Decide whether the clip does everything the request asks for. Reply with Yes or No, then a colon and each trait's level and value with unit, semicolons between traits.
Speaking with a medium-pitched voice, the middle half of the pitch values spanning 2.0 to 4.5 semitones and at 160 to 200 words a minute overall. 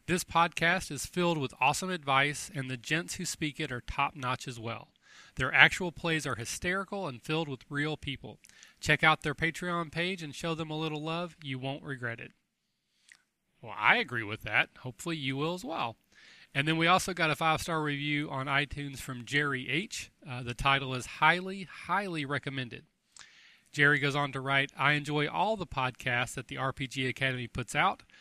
Yes: medium, 145 Hz; average, 3.5 semitones; average, 190 wpm